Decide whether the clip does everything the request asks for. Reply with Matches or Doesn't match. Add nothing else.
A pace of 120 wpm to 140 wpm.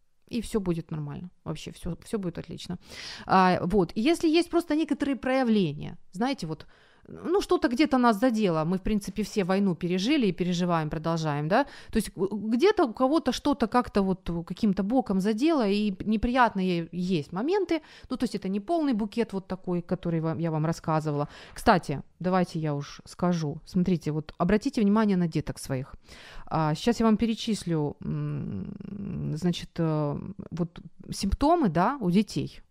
Doesn't match